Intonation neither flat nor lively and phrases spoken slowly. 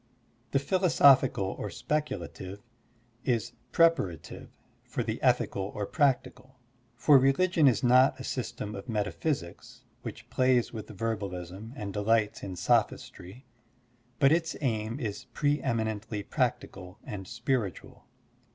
Yes: average, 4.9 semitones; slow, 120 wpm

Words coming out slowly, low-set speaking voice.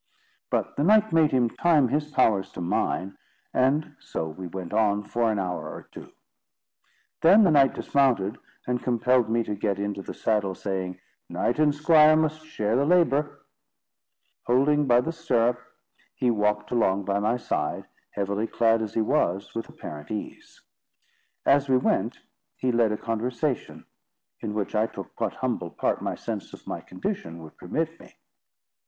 No: average, 165 wpm; low, 115 Hz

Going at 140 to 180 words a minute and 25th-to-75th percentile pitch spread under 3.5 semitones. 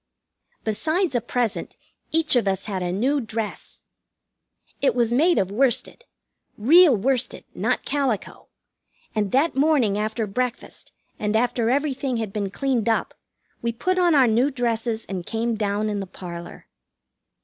No: average, 150 wpm; average, 4.4 semitones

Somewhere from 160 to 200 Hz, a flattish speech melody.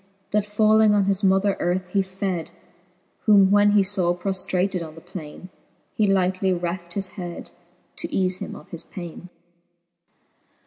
Yes: high, 190 Hz; narrow, 2.1 semitones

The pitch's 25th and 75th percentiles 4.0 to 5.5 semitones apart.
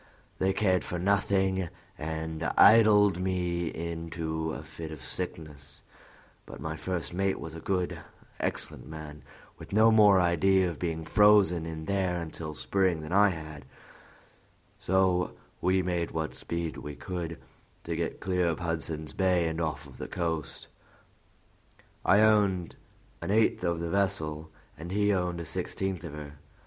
No: average, 2.9 semitones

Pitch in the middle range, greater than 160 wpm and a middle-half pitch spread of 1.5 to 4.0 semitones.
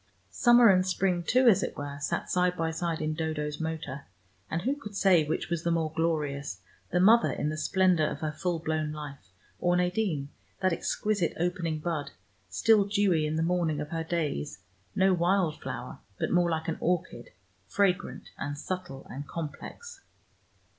Yes: medium, 165 Hz; average, 175 wpm; average, 3.2 semitones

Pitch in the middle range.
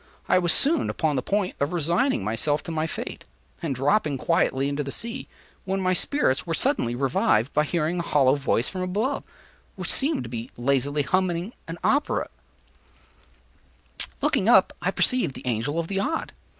Yes: medium, 160 Hz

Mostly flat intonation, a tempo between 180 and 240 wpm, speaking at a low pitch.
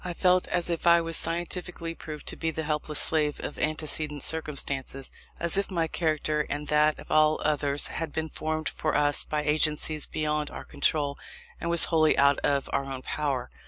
No: narrow, 1.7 semitones; average, 190 wpm; medium, 155 Hz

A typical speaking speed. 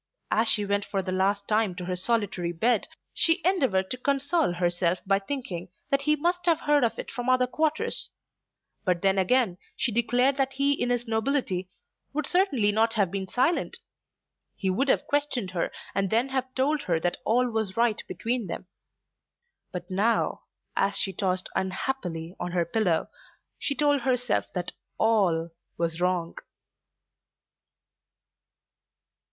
Yes: average, 155 wpm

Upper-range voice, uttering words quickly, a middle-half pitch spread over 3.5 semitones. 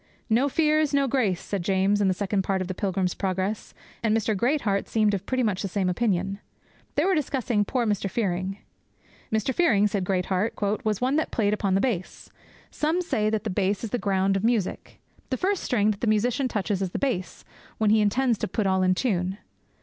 Yes: high, 210 Hz; fast, 210 wpm; average, 4.0 semitones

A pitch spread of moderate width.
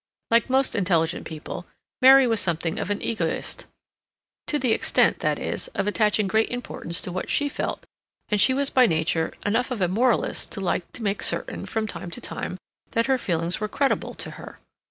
No: wide, 5.7 semitones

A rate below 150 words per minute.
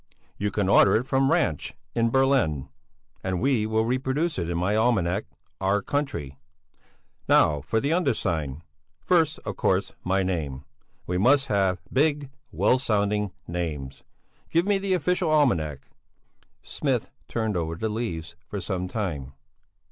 Yes: average, 140 wpm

